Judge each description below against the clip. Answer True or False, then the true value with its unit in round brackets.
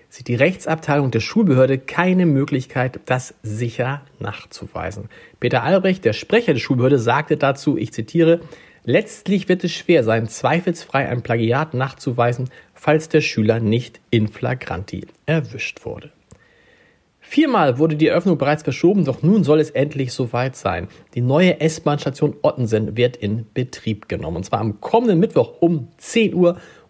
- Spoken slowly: False (145 wpm)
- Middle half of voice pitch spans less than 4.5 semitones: False (5.5 semitones)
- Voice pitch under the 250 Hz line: True (140 Hz)